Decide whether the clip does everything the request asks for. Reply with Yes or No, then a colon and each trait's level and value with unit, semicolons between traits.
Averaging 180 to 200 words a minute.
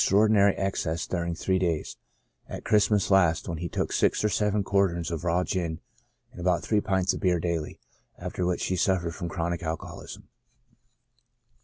No: average, 170 wpm